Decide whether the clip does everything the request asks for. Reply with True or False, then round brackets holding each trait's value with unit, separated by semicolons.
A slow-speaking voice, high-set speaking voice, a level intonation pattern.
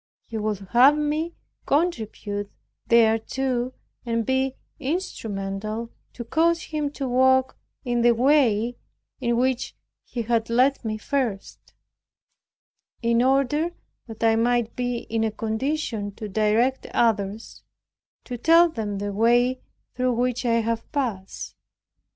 False (125 wpm; 240 Hz; 3.0 semitones)